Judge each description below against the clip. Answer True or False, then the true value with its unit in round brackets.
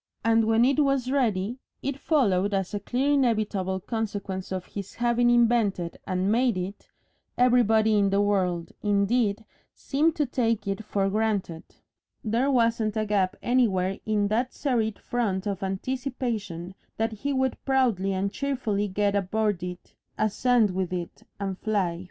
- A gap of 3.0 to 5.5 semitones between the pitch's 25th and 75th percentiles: True (3.9 semitones)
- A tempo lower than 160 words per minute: True (150 wpm)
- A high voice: True (215 Hz)